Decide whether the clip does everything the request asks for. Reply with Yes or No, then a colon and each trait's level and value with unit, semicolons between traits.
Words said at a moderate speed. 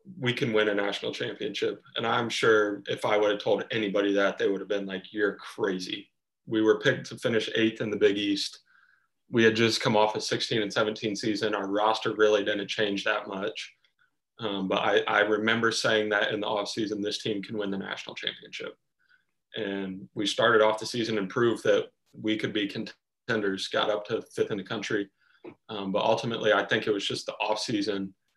No: fast, 210 wpm